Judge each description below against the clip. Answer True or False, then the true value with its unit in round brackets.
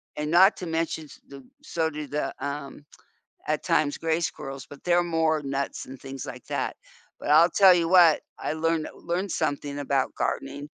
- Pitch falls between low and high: True (155 Hz)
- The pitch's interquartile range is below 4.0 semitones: True (2.8 semitones)